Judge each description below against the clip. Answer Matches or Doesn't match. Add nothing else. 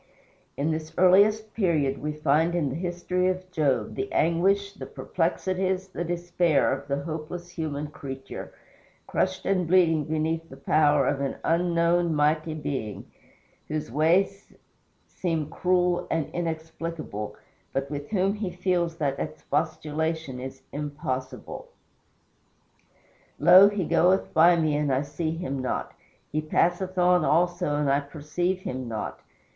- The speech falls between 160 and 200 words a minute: Doesn't match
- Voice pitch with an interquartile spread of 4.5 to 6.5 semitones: Doesn't match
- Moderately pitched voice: Matches